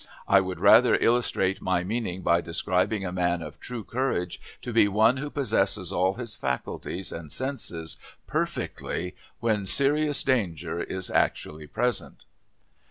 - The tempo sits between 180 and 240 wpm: No, average, 140 wpm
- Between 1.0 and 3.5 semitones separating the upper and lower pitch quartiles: No, average, 5.3 semitones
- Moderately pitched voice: No, very low, 95 Hz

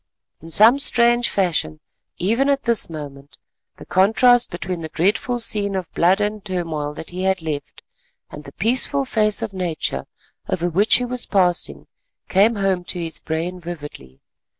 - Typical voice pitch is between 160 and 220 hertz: Yes, medium, 185 Hz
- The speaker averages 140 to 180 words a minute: Yes, average, 160 wpm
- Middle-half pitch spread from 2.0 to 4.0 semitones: No, average, 5.1 semitones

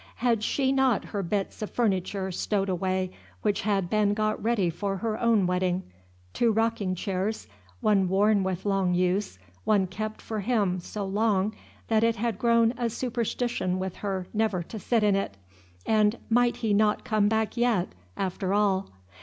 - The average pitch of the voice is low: No, high, 205 Hz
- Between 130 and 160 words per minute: No, average, 170 wpm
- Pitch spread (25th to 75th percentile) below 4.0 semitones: Yes, average, 2.8 semitones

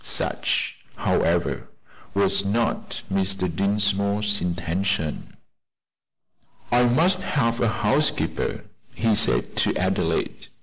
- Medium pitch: No, low, 100 Hz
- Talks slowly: Yes, slow, 90 wpm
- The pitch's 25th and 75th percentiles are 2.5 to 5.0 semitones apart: Yes, average, 3.9 semitones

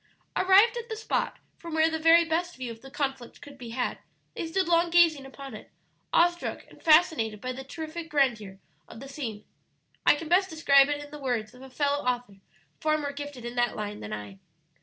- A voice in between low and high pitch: No, very high, 285 Hz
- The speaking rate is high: Yes, fast, 210 wpm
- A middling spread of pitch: Yes, average, 4.9 semitones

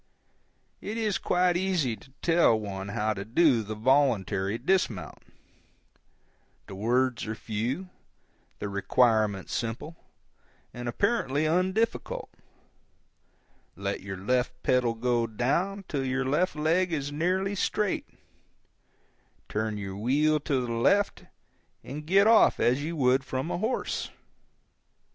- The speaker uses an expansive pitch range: Yes, wide, 7.7 semitones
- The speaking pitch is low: Yes, low, 130 Hz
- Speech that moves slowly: Yes, slow, 120 wpm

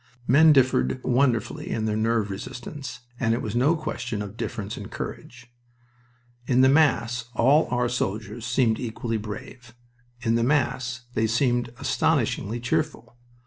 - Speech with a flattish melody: Yes, narrow, 2.3 semitones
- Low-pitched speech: Yes, low, 120 Hz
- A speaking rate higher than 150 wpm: No, average, 145 wpm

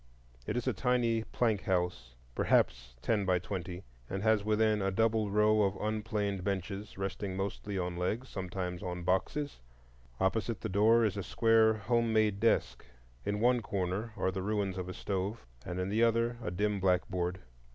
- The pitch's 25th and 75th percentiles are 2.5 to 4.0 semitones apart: Yes, average, 3.0 semitones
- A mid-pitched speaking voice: No, low, 100 Hz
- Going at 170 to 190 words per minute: Yes, average, 175 wpm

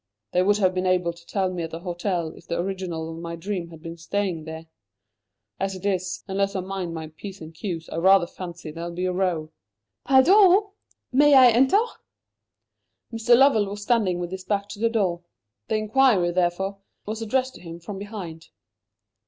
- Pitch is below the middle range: No, medium, 185 Hz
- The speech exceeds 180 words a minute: Yes, average, 190 wpm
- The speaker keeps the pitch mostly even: No, average, 3.4 semitones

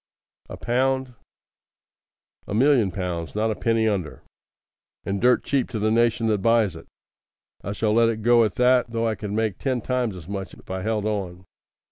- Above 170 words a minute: Yes, average, 185 wpm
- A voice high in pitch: No, low, 110 Hz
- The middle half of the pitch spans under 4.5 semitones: Yes, average, 2.9 semitones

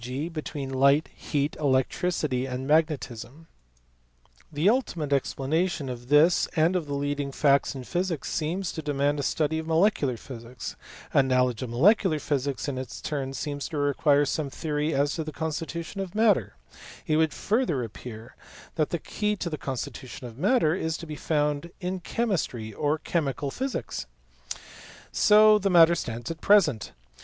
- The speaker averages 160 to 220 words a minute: Yes, average, 165 wpm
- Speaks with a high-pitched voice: No, medium, 150 Hz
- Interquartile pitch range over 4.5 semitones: No, average, 3.9 semitones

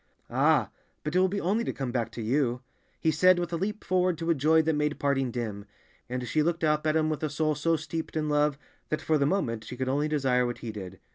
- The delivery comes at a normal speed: No, fast, 260 wpm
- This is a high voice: No, medium, 150 Hz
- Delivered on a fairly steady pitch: No, average, 4.3 semitones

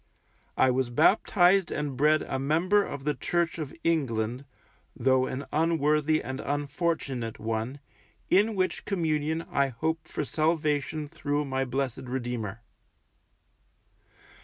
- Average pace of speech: No, slow, 120 wpm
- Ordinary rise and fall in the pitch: Yes, average, 3.6 semitones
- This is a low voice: No, medium, 145 Hz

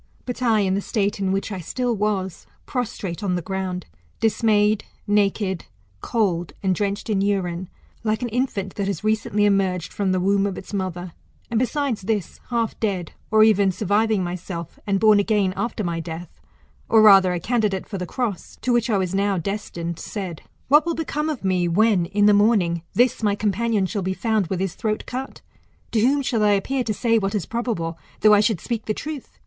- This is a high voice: Yes, high, 205 Hz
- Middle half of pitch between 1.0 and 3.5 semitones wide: Yes, average, 3.0 semitones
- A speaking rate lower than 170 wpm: No, average, 200 wpm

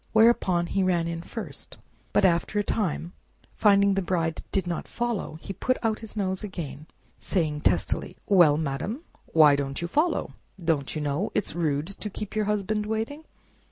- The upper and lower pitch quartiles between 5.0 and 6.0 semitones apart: No, average, 4.5 semitones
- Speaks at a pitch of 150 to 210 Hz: Yes, medium, 185 Hz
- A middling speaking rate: Yes, average, 170 wpm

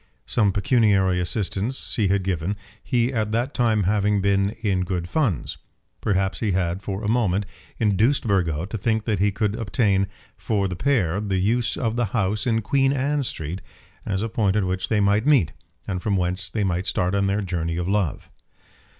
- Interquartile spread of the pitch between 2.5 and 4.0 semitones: Yes, average, 3.1 semitones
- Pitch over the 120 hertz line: No, low, 100 Hz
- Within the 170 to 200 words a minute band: Yes, average, 190 wpm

